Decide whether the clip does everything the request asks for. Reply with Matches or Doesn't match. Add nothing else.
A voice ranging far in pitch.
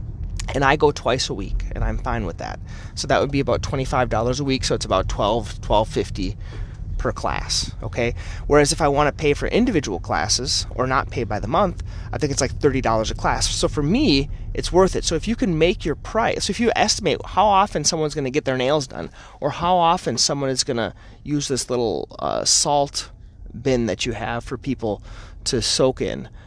Matches